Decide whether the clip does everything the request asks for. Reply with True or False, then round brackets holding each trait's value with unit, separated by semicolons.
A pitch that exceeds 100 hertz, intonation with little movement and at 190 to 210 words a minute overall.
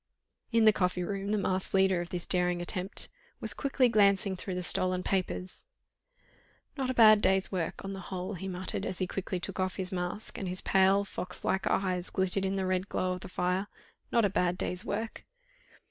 True (190 Hz; 1.5 semitones; 205 wpm)